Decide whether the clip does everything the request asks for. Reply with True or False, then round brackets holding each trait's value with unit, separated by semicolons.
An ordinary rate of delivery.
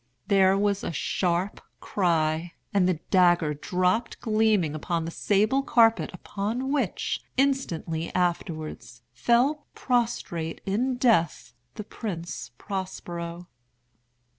False (100 wpm)